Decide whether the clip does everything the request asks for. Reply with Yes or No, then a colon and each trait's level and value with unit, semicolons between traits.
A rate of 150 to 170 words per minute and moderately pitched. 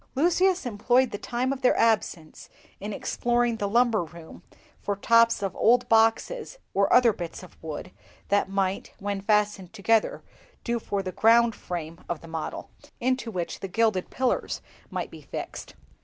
No: average, 160 wpm; high, 215 Hz